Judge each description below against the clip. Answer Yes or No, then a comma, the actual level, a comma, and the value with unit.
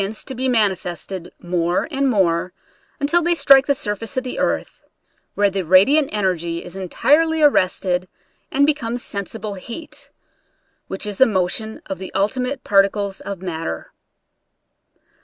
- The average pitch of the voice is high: Yes, high, 205 Hz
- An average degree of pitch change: No, wide, 6.0 semitones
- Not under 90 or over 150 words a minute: Yes, average, 145 wpm